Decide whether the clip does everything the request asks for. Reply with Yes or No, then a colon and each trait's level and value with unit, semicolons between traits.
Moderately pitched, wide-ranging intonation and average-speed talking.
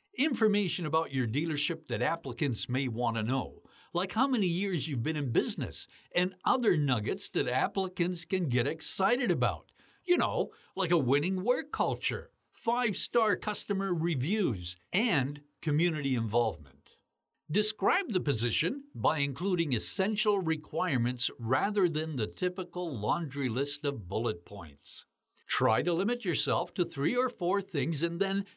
Yes: medium, 170 Hz; wide, 6.4 semitones; average, 145 wpm